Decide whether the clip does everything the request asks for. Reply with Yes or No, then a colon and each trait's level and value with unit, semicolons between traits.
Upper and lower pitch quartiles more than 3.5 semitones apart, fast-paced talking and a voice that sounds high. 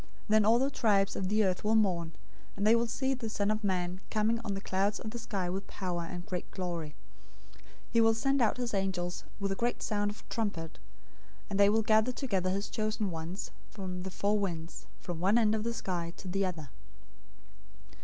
No: average, 3.2 semitones; fast, 215 wpm; high, 200 Hz